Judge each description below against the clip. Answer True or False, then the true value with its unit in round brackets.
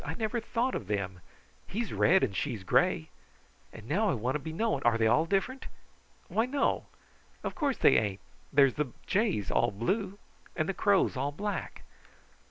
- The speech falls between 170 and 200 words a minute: True (180 wpm)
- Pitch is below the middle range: False (160 Hz)